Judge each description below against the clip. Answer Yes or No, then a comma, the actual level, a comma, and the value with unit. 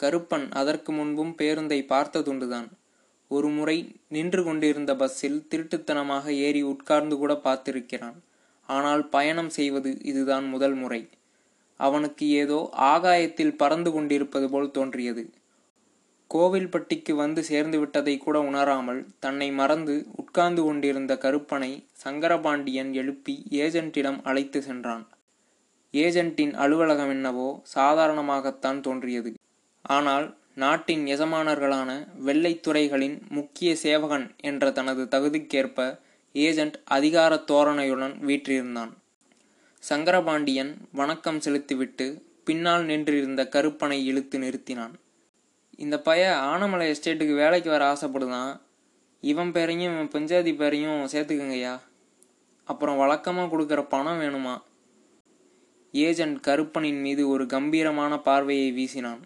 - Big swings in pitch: No, narrow, 2.6 semitones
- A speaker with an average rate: Yes, average, 95 wpm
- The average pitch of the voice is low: No, medium, 145 Hz